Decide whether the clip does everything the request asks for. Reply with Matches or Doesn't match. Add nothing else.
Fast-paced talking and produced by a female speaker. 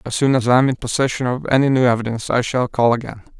Doesn't match